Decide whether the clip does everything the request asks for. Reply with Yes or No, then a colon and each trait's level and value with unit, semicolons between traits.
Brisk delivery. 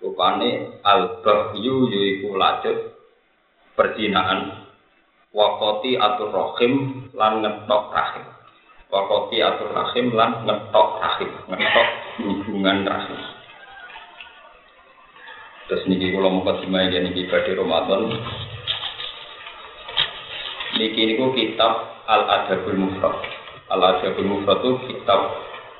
No: average, 100 wpm